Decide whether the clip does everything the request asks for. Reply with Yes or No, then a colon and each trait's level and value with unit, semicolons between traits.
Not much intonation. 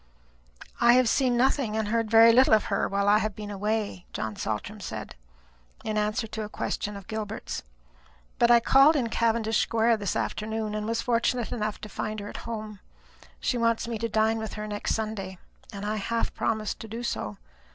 Yes: narrow, 1.7 semitones